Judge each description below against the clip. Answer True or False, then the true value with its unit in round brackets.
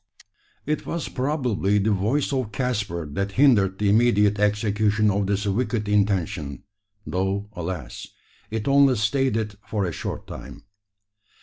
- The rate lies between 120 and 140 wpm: True (135 wpm)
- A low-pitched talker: True (105 Hz)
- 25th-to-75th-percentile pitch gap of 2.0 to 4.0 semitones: True (3.6 semitones)